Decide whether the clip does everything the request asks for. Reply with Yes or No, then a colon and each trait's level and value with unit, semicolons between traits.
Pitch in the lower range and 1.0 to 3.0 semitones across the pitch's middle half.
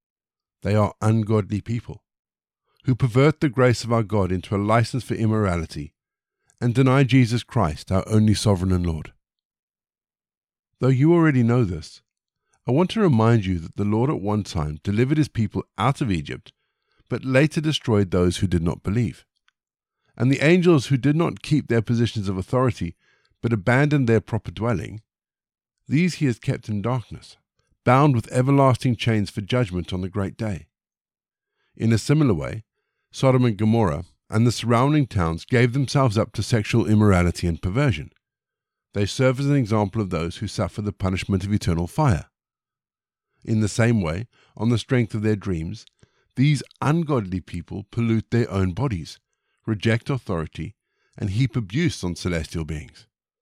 No: low, 110 Hz; average, 4.8 semitones